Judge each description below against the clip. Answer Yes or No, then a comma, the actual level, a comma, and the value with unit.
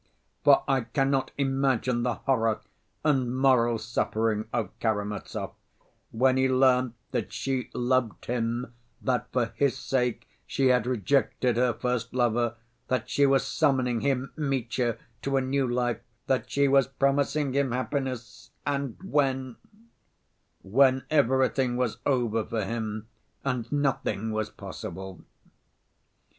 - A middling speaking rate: No, slow, 125 wpm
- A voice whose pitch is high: No, low, 125 Hz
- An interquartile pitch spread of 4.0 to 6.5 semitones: No, narrow, 2.6 semitones